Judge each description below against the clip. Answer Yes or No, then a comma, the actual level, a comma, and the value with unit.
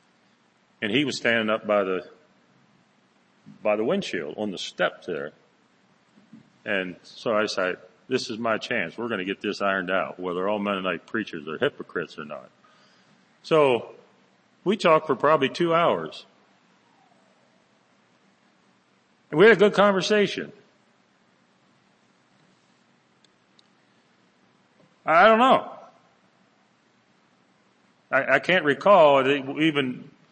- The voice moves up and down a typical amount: No, wide, 8.2 semitones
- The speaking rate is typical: No, slow, 115 wpm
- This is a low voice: Yes, low, 115 Hz